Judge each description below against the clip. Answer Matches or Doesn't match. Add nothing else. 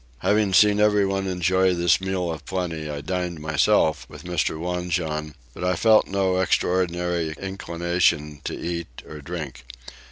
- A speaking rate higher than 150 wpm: Doesn't match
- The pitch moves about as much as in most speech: Matches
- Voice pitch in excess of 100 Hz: Doesn't match